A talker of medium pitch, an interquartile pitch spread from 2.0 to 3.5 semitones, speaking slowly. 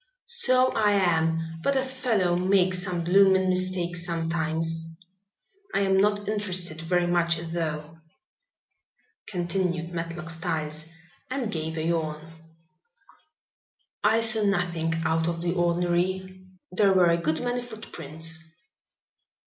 Yes: medium, 175 Hz; average, 2.9 semitones; slow, 115 wpm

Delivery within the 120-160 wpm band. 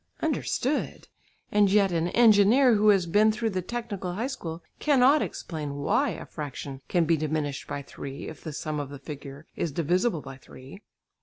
No: average, 175 wpm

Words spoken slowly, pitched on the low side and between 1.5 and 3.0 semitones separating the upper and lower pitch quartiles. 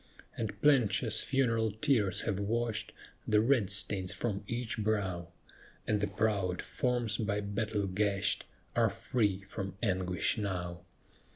Yes: slow, 125 wpm; low, 105 Hz; narrow, 2.6 semitones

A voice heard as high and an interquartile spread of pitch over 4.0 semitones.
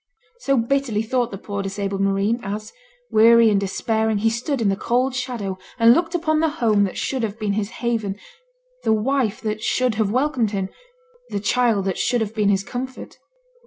No: high, 220 Hz; average, 3.7 semitones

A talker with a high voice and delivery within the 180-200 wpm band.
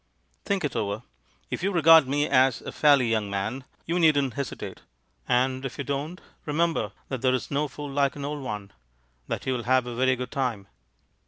No: low, 130 Hz; average, 190 wpm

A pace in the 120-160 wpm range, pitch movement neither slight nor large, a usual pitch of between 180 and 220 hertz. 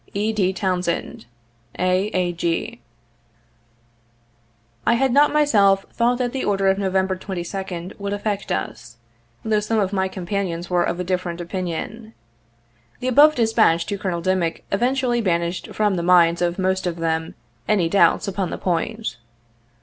Yes: average, 155 wpm; average, 3.5 semitones; high, 190 Hz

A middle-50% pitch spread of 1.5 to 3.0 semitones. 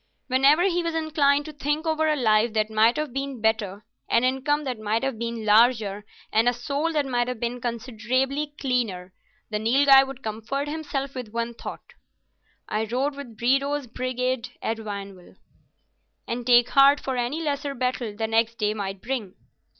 No: average, 4.0 semitones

